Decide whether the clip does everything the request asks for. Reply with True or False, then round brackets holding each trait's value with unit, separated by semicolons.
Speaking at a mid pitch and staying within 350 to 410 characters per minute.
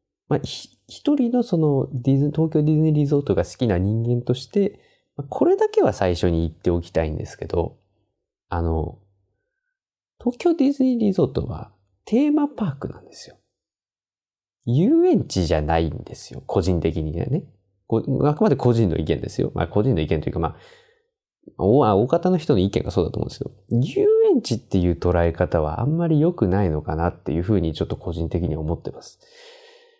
False (120 Hz; 360 characters per minute)